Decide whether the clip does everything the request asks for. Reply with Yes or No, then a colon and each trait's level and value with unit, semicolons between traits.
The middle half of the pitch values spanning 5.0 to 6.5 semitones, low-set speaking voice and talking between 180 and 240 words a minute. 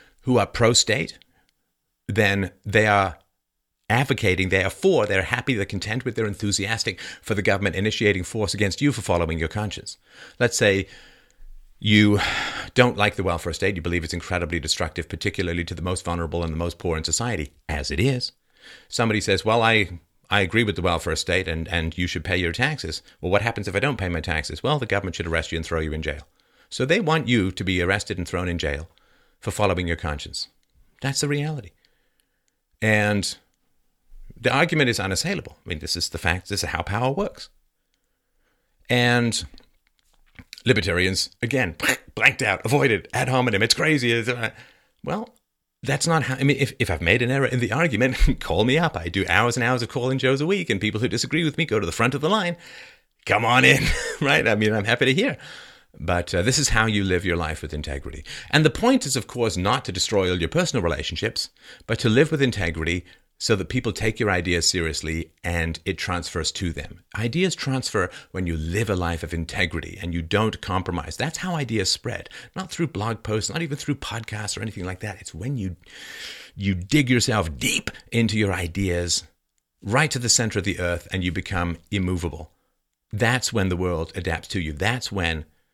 Yes: wide, 5.6 semitones; low, 100 Hz; average, 200 wpm